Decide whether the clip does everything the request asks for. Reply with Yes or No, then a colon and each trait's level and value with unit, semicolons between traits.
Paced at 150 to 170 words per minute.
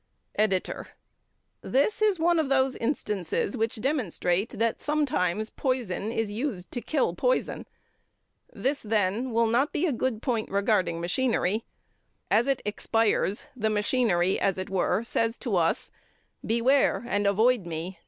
No: average, 140 wpm